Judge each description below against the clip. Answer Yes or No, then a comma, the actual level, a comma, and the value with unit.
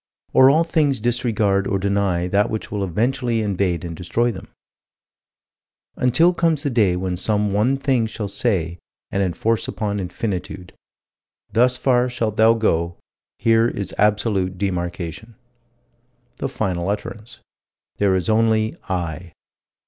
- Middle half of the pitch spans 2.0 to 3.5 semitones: No, average, 4.1 semitones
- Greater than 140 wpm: No, slow, 135 wpm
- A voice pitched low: Yes, low, 105 Hz